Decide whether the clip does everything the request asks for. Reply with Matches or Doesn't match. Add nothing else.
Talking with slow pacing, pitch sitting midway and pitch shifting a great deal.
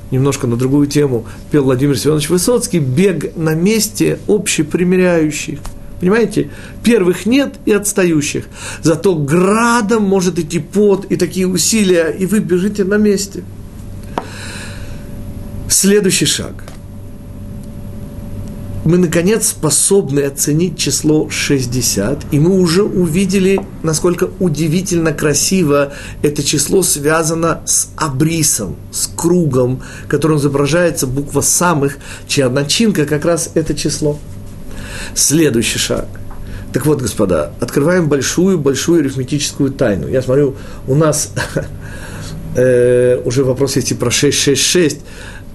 Matches